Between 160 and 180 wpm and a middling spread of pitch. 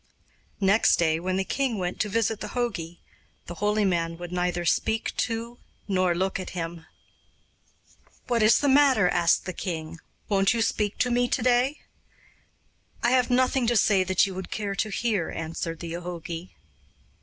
Yes: average, 170 wpm; average, 4.8 semitones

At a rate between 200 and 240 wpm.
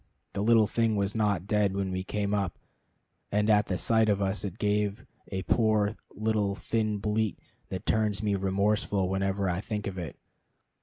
No: average, 175 wpm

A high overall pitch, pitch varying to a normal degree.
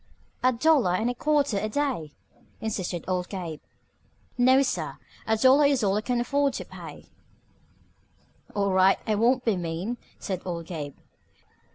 No: high, 215 Hz; wide, 5.9 semitones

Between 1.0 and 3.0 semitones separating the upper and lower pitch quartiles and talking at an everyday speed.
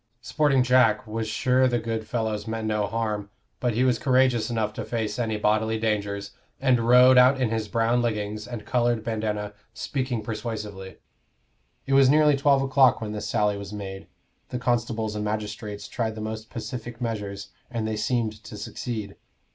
Yes: average, 2.7 semitones; average, 170 wpm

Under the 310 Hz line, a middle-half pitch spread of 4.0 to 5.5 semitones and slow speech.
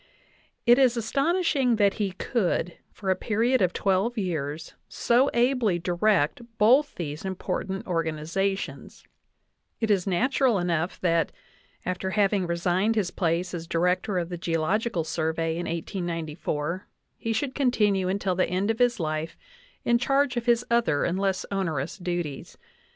No: high, 190 Hz; average, 5.1 semitones; average, 150 wpm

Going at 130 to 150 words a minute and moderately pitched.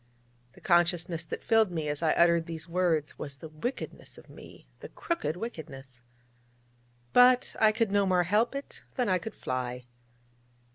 No: average, 160 wpm; medium, 175 Hz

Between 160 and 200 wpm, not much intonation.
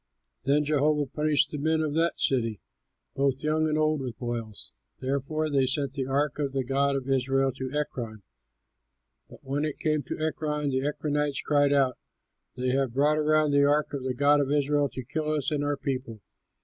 Yes: average, 190 wpm; narrow, 2.1 semitones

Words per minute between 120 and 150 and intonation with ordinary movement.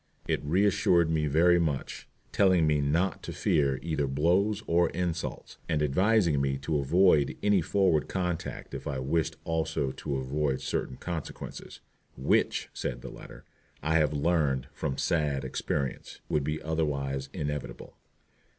Yes: average, 140 wpm; average, 3.8 semitones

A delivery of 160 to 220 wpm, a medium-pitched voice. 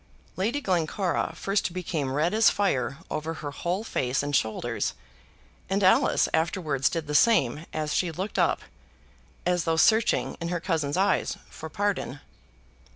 No: average, 150 wpm; medium, 165 Hz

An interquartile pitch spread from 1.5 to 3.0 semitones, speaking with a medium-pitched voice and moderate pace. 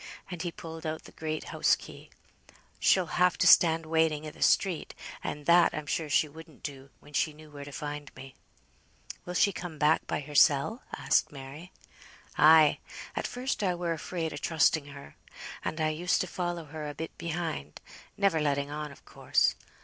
Yes: narrow, 2.6 semitones; medium, 155 Hz; average, 185 wpm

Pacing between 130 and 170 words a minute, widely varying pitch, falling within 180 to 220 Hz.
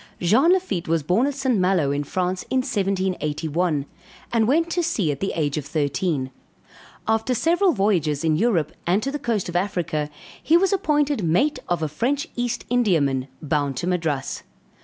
No: average, 180 wpm; wide, 8.5 semitones; medium, 185 Hz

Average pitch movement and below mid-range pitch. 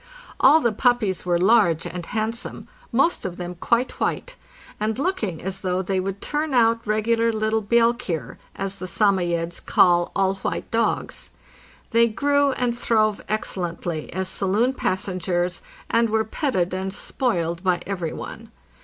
No: average, 4.3 semitones; high, 200 Hz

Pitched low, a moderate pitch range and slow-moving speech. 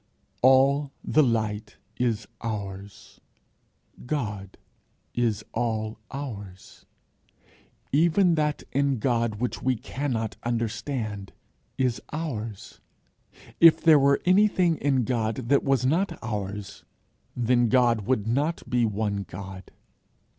Yes: low, 120 Hz; average, 4.7 semitones; slow, 105 wpm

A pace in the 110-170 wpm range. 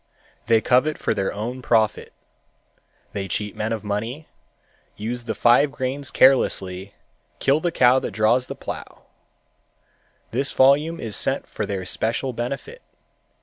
Yes: average, 140 wpm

